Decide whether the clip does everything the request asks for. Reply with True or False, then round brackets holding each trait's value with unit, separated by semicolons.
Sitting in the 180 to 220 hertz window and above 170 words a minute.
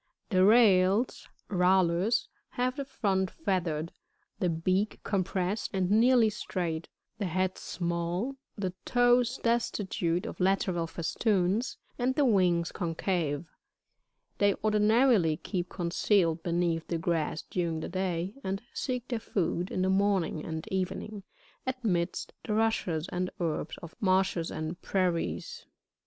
False (185 Hz; 135 wpm)